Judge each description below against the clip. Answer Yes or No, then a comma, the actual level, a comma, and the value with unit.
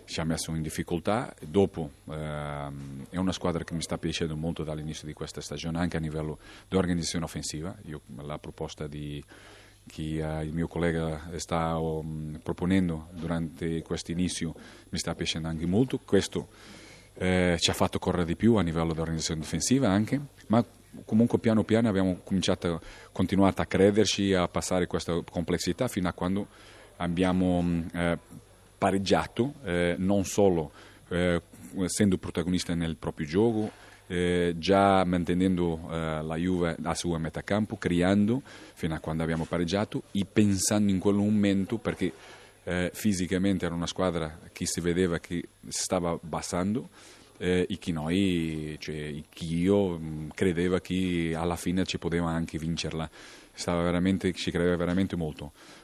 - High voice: No, very low, 90 Hz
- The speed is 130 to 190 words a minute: Yes, average, 150 wpm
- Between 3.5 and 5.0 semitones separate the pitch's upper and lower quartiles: No, average, 2.8 semitones